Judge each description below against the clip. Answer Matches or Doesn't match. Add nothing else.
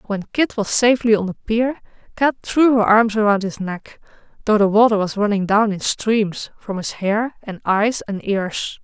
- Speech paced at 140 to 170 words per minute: Doesn't match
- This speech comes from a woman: Matches